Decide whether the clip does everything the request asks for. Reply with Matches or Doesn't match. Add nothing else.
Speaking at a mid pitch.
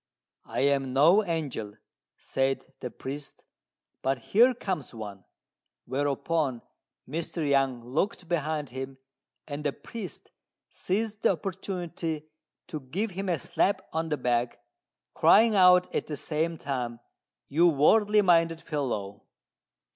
Matches